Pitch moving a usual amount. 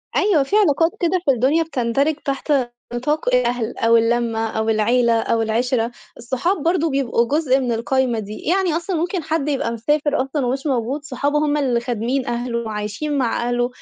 Yes: average, 4.2 semitones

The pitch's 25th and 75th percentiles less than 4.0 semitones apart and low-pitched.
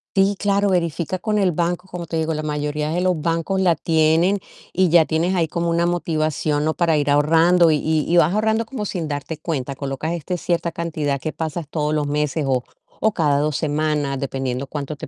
No: average, 2.8 semitones; medium, 160 Hz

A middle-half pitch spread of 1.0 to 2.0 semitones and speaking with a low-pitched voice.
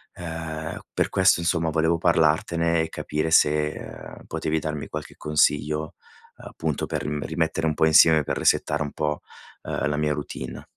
Yes: narrow, 1.3 semitones; very low, 80 Hz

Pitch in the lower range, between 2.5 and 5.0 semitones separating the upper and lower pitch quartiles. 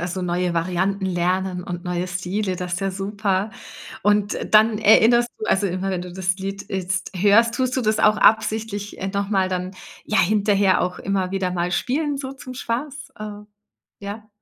No: high, 195 Hz; average, 2.8 semitones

